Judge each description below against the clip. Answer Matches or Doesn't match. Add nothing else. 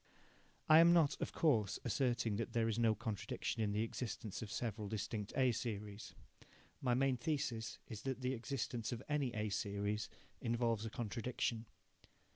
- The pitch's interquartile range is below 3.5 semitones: Matches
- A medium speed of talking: Matches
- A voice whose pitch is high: Doesn't match